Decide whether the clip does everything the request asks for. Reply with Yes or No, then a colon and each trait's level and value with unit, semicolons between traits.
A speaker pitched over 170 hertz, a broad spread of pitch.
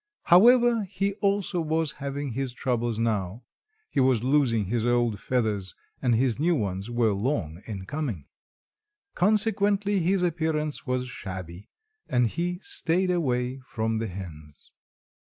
No: low, 125 Hz; wide, 7.4 semitones